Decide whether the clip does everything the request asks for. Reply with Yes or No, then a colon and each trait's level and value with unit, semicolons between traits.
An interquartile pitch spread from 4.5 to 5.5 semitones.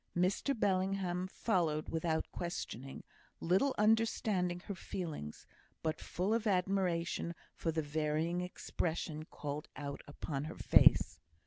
No: average, 3.6 semitones